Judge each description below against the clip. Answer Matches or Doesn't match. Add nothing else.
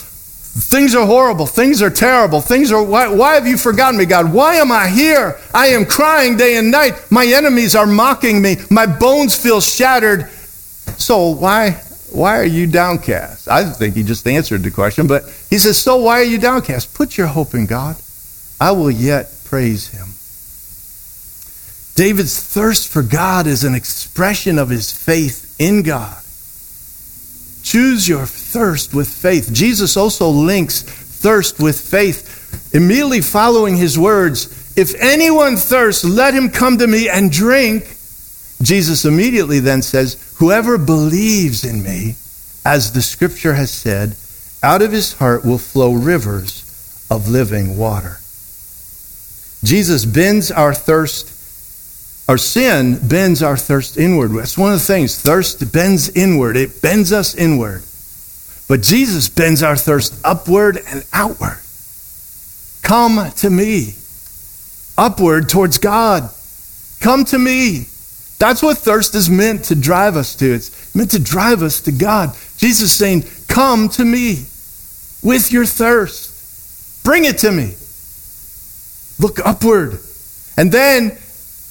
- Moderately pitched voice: Matches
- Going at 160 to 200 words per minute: Doesn't match